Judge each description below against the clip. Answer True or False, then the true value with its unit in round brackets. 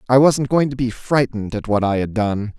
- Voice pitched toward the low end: True (120 Hz)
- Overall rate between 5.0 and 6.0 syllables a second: True (5.4 syllables/s)